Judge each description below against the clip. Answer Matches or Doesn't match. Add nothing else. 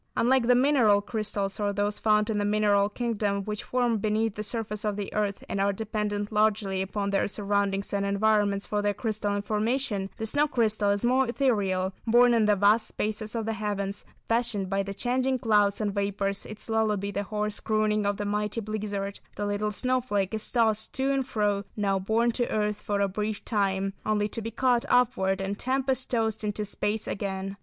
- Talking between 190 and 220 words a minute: Matches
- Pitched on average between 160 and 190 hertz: Doesn't match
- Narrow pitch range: Matches